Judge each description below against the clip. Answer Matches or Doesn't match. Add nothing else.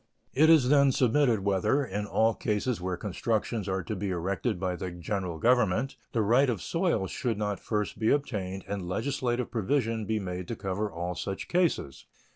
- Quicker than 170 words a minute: Matches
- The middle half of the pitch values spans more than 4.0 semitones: Matches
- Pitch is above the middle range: Doesn't match